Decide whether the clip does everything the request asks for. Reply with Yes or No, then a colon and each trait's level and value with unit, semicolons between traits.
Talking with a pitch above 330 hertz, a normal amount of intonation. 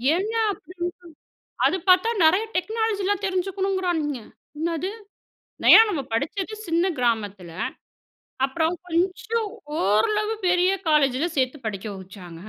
No: very high, 350 Hz; wide, 7.0 semitones